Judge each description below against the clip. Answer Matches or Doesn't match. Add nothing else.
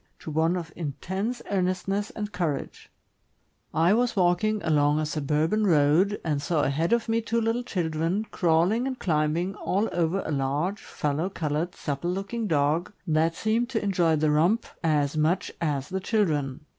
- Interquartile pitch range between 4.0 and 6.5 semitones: Matches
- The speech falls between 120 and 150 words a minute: Doesn't match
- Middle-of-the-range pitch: Matches